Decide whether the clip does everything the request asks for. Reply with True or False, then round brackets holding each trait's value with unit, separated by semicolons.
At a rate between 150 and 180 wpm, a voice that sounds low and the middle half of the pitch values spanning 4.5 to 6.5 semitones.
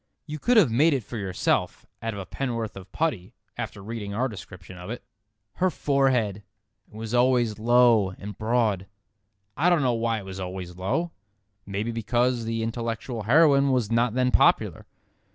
False (170 wpm; 115 Hz; 3.9 semitones)